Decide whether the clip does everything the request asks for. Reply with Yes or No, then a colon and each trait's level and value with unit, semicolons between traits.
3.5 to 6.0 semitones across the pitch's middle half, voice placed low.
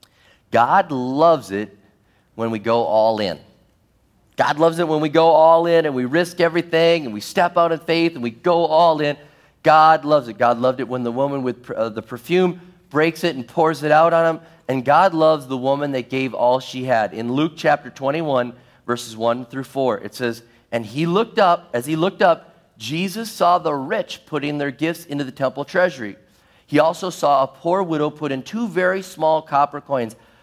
No: average, 5.1 semitones; medium, 145 Hz